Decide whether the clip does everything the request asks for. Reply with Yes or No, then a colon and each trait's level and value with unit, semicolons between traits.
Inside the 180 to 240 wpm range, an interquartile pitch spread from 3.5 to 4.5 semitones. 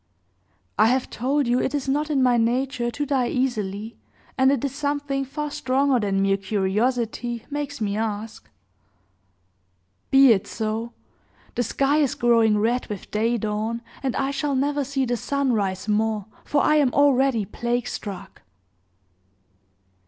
No: average, 150 wpm; average, 4.0 semitones